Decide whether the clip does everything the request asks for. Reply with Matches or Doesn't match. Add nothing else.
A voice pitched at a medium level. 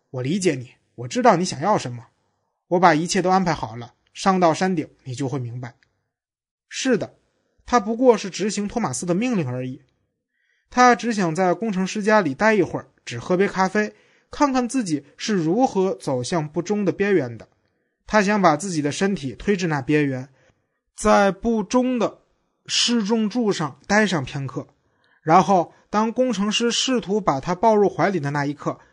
Matches